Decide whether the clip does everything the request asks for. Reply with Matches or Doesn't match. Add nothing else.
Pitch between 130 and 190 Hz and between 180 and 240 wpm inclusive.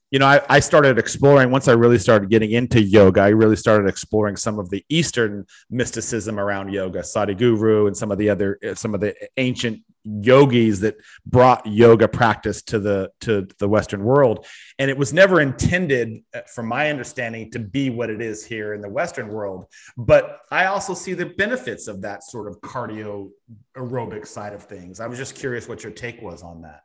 Doesn't match